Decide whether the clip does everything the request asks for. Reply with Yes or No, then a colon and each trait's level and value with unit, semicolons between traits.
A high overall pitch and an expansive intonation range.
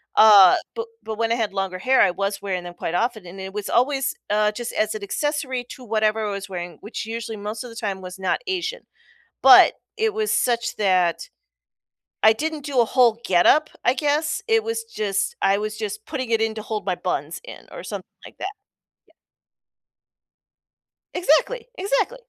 Yes: high, 220 Hz; wide, 6.5 semitones